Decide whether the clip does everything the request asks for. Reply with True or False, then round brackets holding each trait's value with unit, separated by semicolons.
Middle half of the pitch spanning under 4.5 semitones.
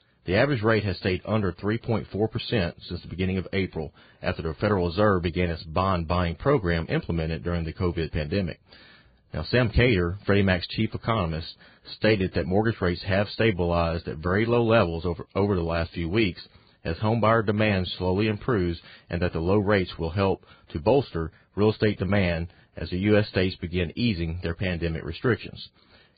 True (3.9 semitones)